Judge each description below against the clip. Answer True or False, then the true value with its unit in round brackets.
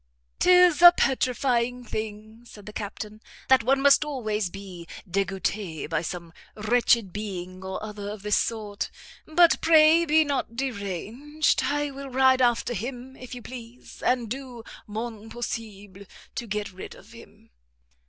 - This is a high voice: True (230 Hz)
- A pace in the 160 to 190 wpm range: False (145 wpm)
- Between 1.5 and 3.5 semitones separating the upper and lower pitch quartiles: False (4.4 semitones)